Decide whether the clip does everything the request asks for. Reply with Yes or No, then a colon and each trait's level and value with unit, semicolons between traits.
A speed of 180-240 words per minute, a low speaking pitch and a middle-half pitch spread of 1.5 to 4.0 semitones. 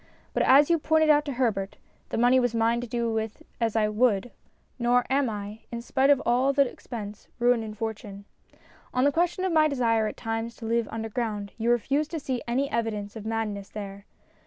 No: fast, 205 wpm; high, 235 Hz; average, 3.3 semitones